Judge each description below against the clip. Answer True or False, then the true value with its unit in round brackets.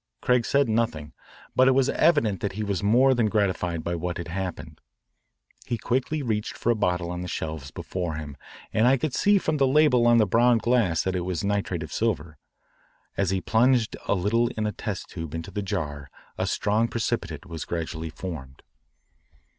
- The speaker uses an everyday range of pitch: False (5.7 semitones)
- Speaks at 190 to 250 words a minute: True (195 wpm)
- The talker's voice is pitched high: False (100 Hz)